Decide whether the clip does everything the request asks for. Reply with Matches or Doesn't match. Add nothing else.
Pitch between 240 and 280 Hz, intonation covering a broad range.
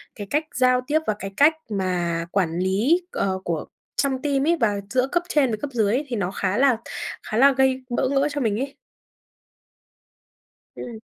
Matches